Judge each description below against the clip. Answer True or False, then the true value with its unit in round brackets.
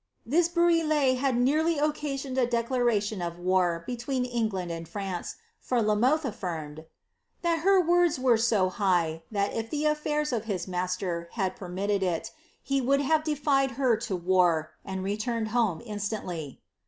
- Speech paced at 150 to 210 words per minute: True (165 wpm)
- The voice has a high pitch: True (230 Hz)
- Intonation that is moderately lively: False (6.7 semitones)